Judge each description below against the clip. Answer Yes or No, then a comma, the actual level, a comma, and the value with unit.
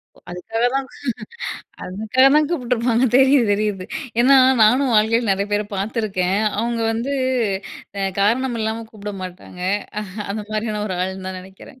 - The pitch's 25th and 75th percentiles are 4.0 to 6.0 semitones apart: No, average, 3.6 semitones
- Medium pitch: No, high, 220 Hz